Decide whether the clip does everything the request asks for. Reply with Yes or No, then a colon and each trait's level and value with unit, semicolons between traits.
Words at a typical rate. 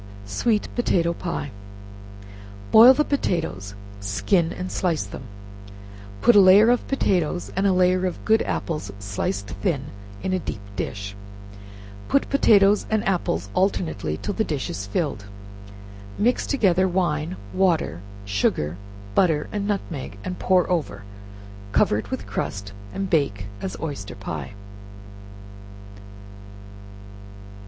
No: slow, 125 wpm